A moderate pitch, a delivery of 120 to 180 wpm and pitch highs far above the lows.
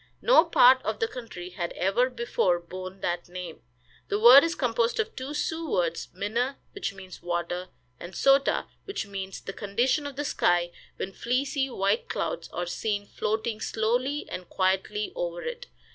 No: high, 215 Hz; average, 165 wpm; wide, 6.2 semitones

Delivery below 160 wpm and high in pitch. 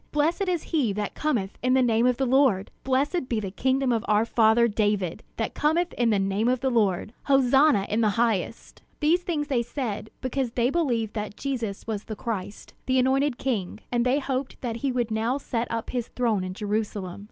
No: fast, 205 wpm; high, 240 Hz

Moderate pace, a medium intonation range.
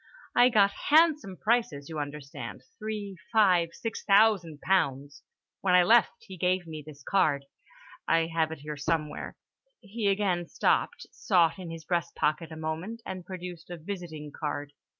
Yes: average, 150 wpm; average, 4.3 semitones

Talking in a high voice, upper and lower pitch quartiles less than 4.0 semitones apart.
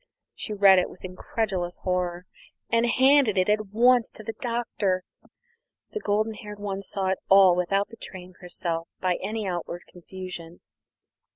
Yes: high, 195 Hz; average, 3.1 semitones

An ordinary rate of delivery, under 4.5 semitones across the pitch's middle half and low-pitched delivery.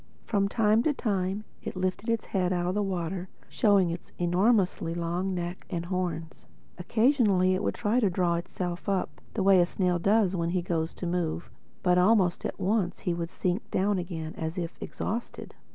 No: average, 185 wpm; narrow, 2.5 semitones; medium, 185 Hz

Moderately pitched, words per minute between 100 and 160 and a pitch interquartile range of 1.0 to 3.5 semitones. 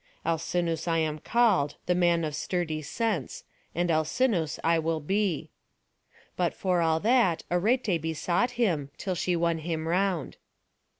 Yes: medium, 170 Hz; average, 140 wpm; average, 2.9 semitones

